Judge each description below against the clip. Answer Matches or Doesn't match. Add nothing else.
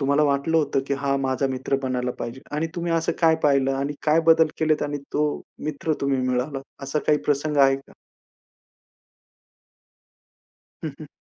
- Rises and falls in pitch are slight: Matches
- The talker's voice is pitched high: Doesn't match